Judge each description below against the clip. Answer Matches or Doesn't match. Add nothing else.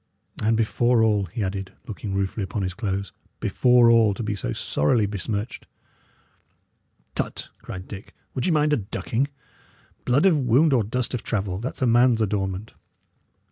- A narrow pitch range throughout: Doesn't match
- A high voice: Doesn't match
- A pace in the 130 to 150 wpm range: Doesn't match